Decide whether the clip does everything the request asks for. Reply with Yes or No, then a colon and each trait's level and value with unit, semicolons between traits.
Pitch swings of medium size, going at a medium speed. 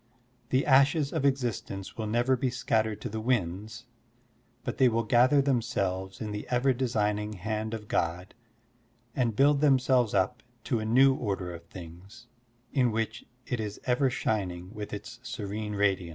Yes: average, 3.8 semitones; average, 160 wpm